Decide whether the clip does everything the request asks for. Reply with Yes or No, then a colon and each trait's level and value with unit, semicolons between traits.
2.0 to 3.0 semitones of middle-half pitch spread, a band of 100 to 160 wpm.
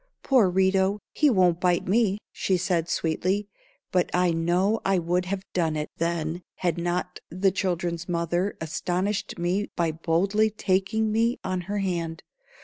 Yes: narrow, 2.4 semitones; average, 150 wpm